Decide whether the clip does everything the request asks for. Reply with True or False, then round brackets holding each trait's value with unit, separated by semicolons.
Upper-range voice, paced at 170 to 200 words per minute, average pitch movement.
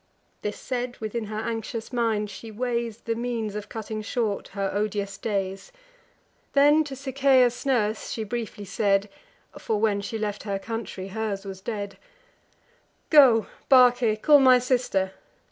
False (220 Hz; 145 wpm; 3.0 semitones)